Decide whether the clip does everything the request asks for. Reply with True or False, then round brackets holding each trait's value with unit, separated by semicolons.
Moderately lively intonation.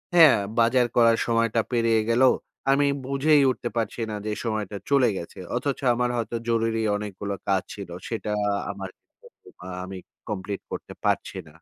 True (3.0 semitones)